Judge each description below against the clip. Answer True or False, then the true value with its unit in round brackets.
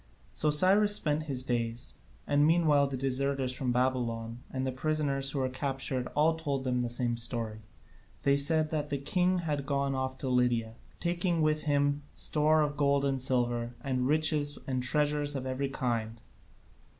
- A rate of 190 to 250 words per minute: False (165 wpm)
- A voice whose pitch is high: False (140 Hz)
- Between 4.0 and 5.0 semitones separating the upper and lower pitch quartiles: False (2.9 semitones)